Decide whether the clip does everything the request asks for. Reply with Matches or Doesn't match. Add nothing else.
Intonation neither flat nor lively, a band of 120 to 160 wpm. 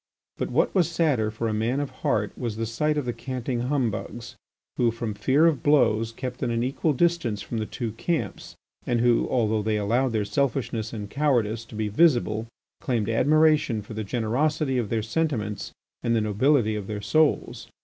Doesn't match